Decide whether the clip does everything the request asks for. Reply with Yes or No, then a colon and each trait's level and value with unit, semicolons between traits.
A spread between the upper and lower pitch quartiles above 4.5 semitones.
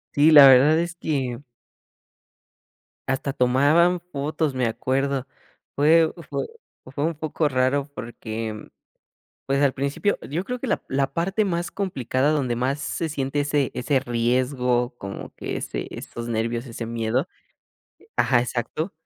No: average, 3.8 semitones